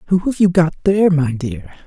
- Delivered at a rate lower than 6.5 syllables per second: Yes, 5.7 syllables/s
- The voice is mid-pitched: Yes, medium, 170 Hz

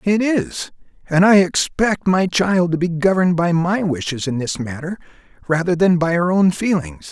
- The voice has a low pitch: No, medium, 175 Hz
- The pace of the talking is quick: No, average, 185 wpm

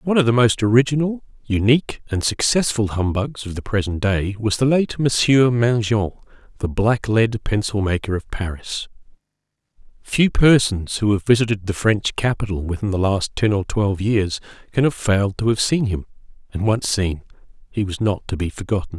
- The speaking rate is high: No, average, 175 wpm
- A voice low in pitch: Yes, low, 110 Hz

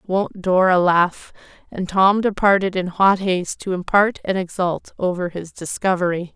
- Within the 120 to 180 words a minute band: Yes, average, 150 wpm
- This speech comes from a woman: Yes, female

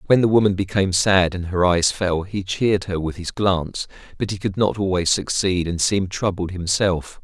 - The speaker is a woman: No, male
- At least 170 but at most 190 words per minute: No, fast, 205 wpm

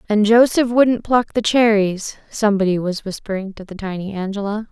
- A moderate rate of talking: Yes, average, 165 wpm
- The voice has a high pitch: Yes, high, 210 Hz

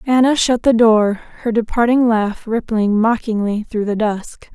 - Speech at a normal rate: Yes, average, 160 wpm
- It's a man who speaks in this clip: No, female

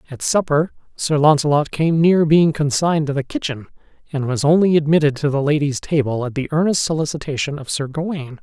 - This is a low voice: No, medium, 150 Hz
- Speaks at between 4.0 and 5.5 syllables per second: No, 5.7 syllables/s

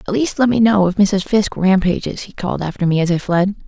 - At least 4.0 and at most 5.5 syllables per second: No, 6.2 syllables/s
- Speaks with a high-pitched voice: Yes, high, 195 Hz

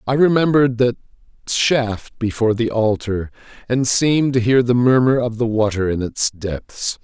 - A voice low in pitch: Yes, low, 120 Hz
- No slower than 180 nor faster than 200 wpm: No, average, 160 wpm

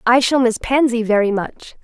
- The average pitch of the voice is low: No, high, 240 Hz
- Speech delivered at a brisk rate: No, average, 195 wpm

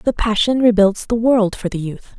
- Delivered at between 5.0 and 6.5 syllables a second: No, 4.8 syllables/s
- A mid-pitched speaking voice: No, high, 215 Hz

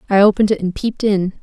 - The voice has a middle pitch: No, high, 200 Hz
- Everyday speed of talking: No, fast, 255 wpm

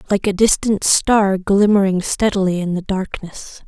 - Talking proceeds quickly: No, average, 145 wpm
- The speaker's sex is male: No, female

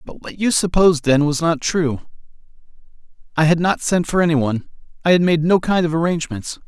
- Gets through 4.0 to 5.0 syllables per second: No, 5.8 syllables/s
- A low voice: No, medium, 160 Hz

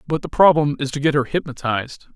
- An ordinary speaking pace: No, fast, 220 wpm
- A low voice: No, medium, 145 Hz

